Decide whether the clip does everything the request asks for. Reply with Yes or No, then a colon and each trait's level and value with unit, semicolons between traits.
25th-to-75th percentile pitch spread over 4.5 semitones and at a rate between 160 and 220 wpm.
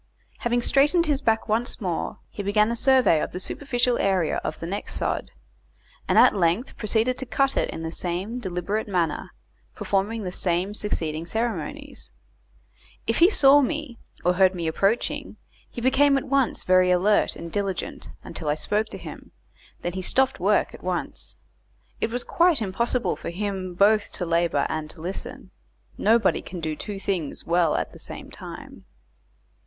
Yes: wide, 5.4 semitones; average, 170 wpm